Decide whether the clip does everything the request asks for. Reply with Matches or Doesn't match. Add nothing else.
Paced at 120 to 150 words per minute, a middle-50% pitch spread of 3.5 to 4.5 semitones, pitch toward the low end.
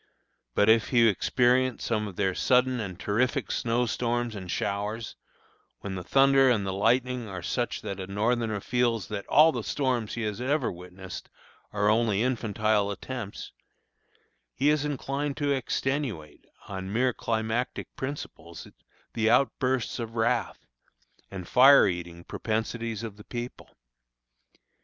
Matches